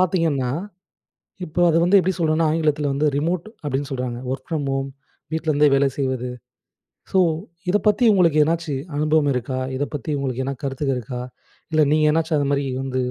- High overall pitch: No, medium, 145 Hz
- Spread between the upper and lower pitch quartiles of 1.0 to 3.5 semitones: Yes, average, 3.0 semitones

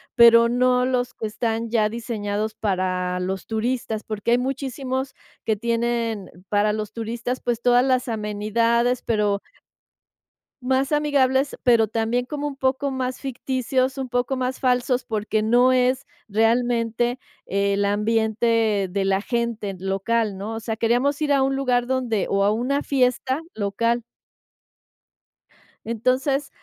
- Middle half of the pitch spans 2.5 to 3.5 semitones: Yes, average, 3.0 semitones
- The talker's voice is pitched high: Yes, high, 235 Hz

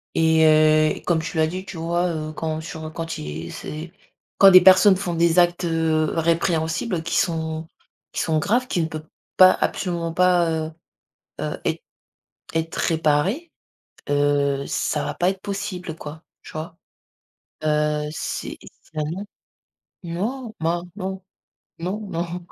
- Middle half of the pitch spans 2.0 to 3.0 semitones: Yes, narrow, 2.5 semitones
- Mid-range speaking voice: Yes, medium, 165 Hz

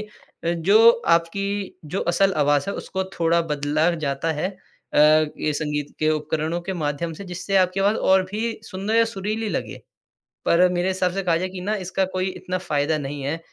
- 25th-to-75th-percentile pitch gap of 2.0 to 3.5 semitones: No, average, 4.0 semitones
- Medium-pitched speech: Yes, medium, 180 Hz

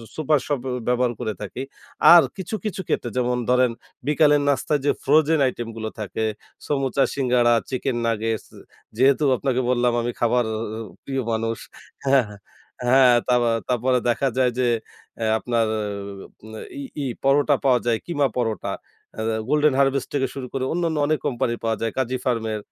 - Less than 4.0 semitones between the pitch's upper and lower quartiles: Yes, average, 2.9 semitones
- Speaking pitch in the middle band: No, low, 125 Hz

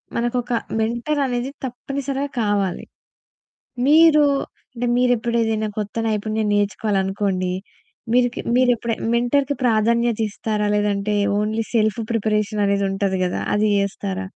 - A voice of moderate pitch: No, high, 220 Hz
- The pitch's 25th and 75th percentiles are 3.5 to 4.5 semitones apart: No, average, 3.0 semitones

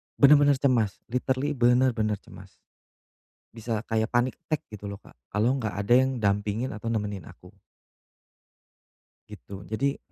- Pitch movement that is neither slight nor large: Yes, average, 3.8 semitones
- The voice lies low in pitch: Yes, low, 115 Hz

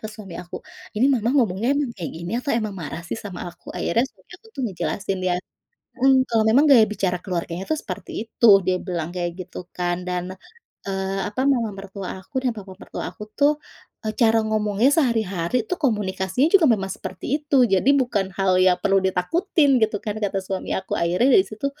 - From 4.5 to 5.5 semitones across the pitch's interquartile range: Yes, average, 4.9 semitones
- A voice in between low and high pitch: No, high, 210 Hz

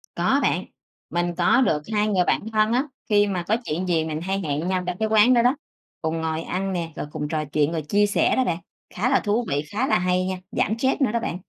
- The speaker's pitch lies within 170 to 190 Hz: Yes, medium, 185 Hz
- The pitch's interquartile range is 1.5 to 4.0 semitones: No, average, 4.7 semitones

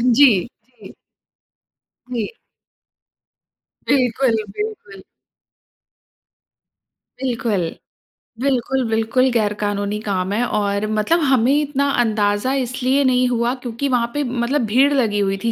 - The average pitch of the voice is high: Yes, high, 240 Hz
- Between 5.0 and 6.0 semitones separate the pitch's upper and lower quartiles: No, average, 3.8 semitones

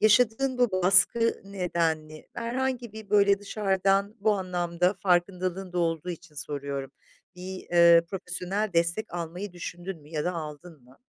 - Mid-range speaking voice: Yes, medium, 180 Hz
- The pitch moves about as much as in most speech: Yes, average, 3.1 semitones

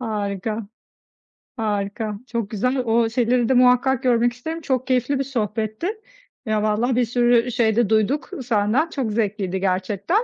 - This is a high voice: Yes, high, 230 Hz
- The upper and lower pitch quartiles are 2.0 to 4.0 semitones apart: Yes, average, 3.0 semitones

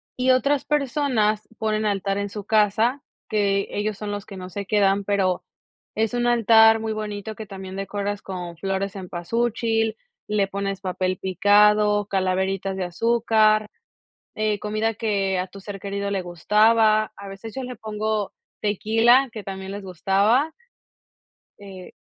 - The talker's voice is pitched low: No, high, 205 Hz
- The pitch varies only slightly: Yes, narrow, 2.1 semitones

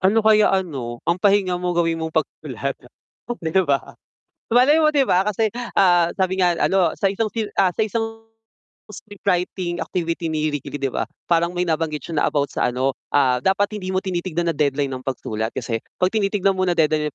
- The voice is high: No, medium, 175 Hz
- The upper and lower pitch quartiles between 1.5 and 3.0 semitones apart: No, average, 4.2 semitones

